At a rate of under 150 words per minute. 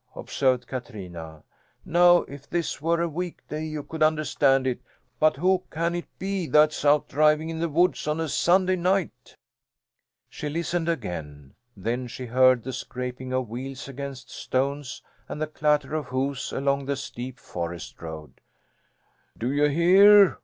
No: average, 155 wpm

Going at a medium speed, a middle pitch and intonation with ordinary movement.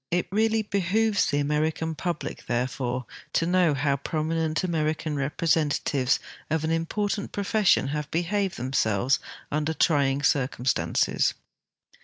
No: slow, 120 wpm; medium, 155 Hz; average, 4.2 semitones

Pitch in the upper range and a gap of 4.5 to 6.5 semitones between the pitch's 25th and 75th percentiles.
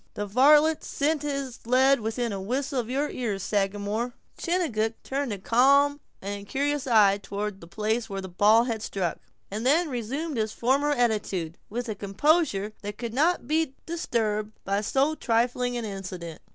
Yes: high, 235 Hz; average, 5.1 semitones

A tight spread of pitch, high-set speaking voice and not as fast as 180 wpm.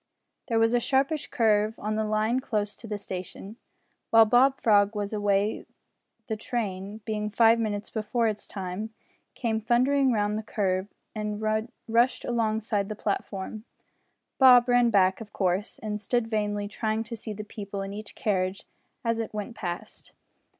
Yes: narrow, 1.9 semitones; high, 215 Hz; average, 160 wpm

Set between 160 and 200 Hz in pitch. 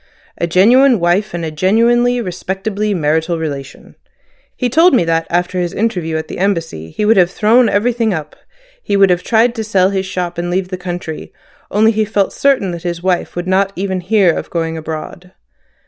Yes: medium, 185 Hz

